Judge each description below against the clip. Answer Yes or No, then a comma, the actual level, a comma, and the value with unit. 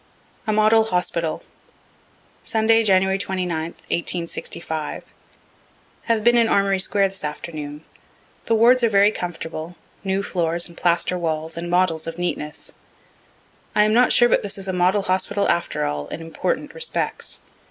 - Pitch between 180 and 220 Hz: Yes, medium, 185 Hz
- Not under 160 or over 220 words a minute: No, average, 145 wpm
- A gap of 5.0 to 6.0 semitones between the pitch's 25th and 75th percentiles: No, average, 4.1 semitones